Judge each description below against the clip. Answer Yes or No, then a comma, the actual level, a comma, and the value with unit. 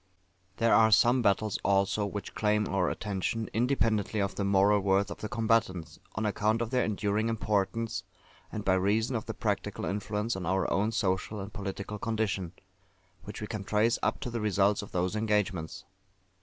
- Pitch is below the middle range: Yes, low, 105 Hz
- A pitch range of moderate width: No, narrow, 2.1 semitones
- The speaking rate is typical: Yes, average, 175 wpm